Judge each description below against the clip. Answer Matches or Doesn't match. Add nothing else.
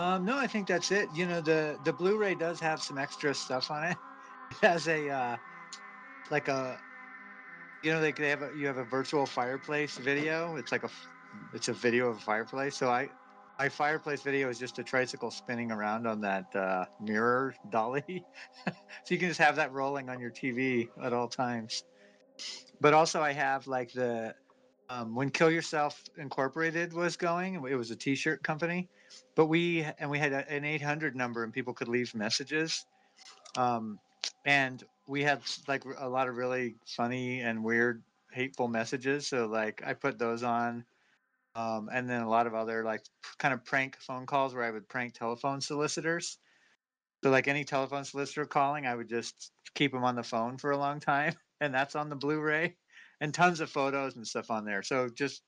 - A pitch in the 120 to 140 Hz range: Matches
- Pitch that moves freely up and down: Doesn't match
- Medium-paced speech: Matches